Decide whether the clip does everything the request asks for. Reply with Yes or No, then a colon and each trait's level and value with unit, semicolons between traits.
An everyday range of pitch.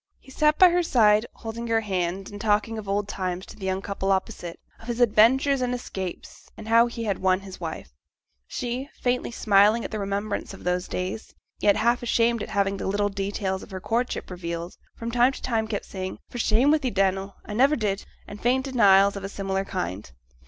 Yes: average, 3.5 semitones